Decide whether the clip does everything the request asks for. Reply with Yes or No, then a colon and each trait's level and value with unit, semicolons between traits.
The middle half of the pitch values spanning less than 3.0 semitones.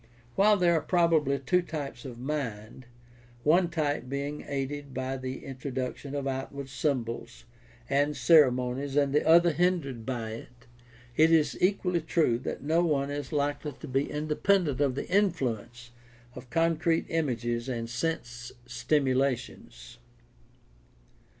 No: average, 4.1 semitones